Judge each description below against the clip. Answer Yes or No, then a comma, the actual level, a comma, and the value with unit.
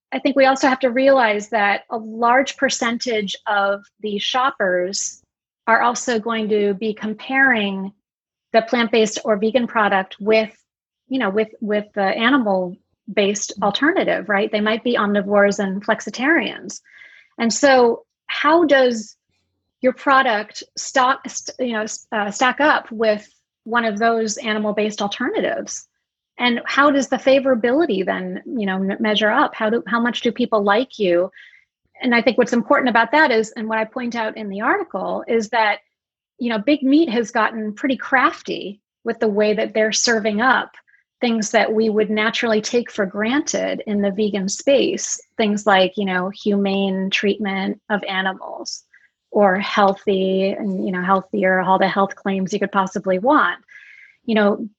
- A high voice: Yes, high, 220 Hz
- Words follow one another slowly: No, average, 160 wpm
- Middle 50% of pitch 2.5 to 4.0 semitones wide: Yes, average, 3.6 semitones